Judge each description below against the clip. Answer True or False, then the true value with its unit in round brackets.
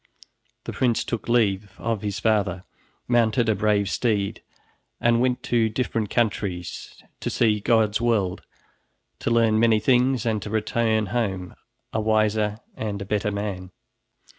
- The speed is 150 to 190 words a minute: False (140 wpm)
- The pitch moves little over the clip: True (2.3 semitones)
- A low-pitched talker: True (110 Hz)